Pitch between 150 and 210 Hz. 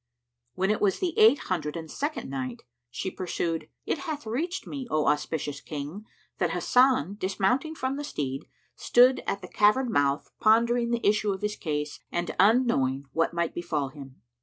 Yes: high, 190 Hz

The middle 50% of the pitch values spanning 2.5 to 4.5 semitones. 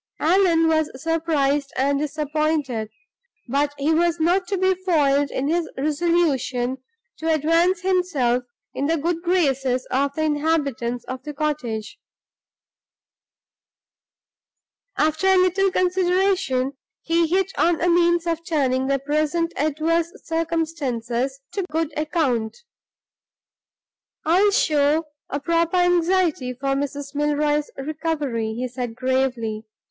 Yes: average, 3.7 semitones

